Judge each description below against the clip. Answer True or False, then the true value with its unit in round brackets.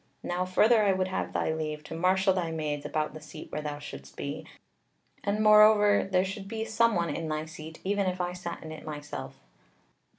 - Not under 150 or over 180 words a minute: False (200 wpm)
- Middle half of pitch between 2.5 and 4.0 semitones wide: False (4.4 semitones)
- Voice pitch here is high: False (180 Hz)